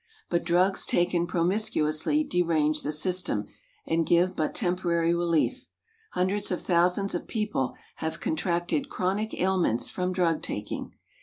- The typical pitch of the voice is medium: Yes, medium, 175 Hz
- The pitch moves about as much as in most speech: No, narrow, 2.1 semitones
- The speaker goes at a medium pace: No, slow, 130 wpm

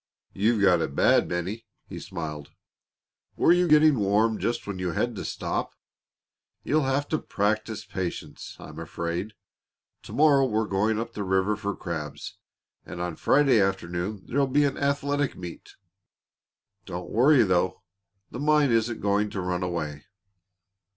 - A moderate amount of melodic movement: No, wide, 6.6 semitones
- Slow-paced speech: No, average, 150 wpm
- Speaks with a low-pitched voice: Yes, low, 105 Hz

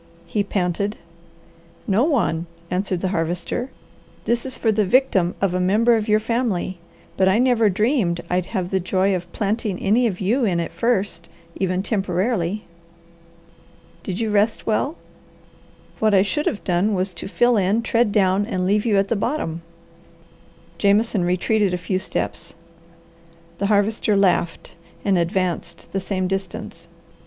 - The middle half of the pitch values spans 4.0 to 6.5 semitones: No, average, 3.3 semitones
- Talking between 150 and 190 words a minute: Yes, average, 155 wpm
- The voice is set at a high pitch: Yes, high, 200 Hz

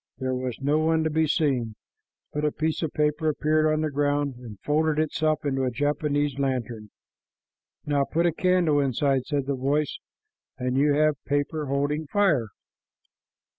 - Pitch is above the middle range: No, medium, 145 Hz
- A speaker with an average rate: Yes, average, 165 wpm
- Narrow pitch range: Yes, narrow, 2.3 semitones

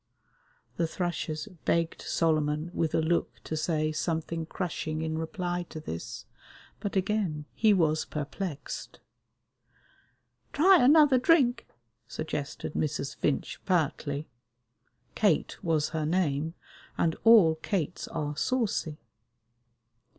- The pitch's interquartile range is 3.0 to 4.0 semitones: Yes, average, 3.6 semitones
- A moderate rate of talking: No, slow, 105 wpm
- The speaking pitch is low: No, medium, 160 Hz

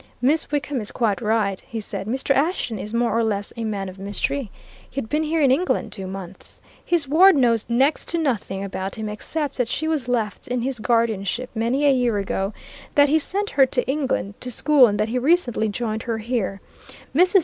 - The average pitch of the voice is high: Yes, high, 240 Hz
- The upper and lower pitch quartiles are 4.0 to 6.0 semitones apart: Yes, average, 5.0 semitones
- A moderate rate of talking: No, fast, 210 wpm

